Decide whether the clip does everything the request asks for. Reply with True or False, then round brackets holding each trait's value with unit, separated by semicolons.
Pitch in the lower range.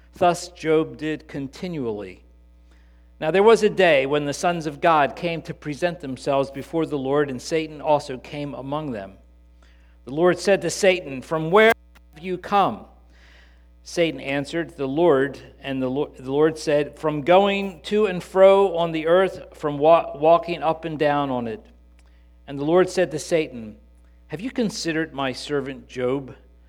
False (150 Hz)